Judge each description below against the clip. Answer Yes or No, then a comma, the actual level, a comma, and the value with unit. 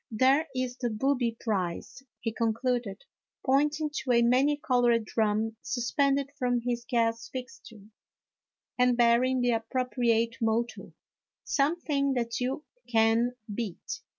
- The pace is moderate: No, slow, 125 wpm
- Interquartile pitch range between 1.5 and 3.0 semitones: Yes, narrow, 2.5 semitones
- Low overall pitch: No, high, 245 Hz